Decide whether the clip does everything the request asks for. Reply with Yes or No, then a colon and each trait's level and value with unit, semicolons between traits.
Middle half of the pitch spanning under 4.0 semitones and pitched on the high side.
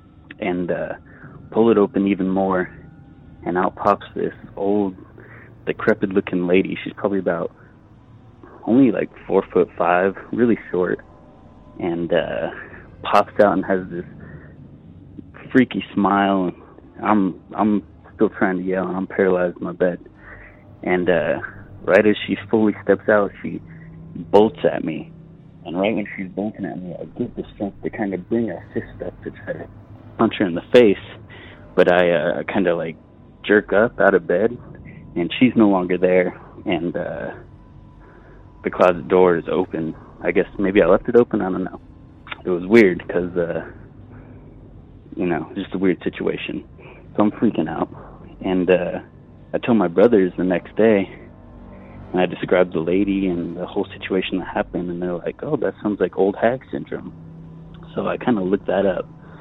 No: average, 2.7 semitones; very low, 95 Hz